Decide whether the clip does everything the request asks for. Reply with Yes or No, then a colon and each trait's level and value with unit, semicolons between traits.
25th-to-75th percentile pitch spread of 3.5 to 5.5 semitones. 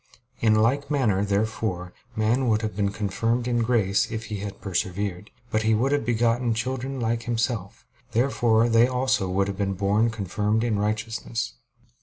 No: narrow, 2.6 semitones